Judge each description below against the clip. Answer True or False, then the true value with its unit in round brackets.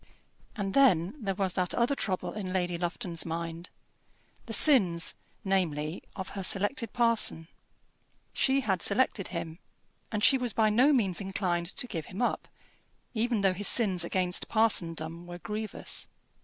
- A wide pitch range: False (4.4 semitones)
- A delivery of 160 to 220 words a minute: False (150 wpm)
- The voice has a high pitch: True (195 Hz)